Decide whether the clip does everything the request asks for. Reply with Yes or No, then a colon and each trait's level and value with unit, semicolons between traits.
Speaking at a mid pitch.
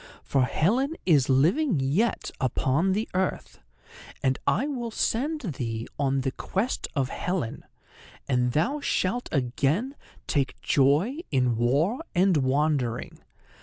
Yes: medium, 150 Hz